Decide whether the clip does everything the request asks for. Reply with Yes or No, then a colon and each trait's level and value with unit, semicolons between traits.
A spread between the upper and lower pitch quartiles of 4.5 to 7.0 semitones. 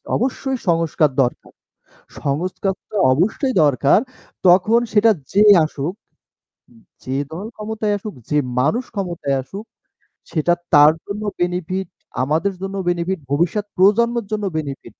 Yes: average, 5.2 semitones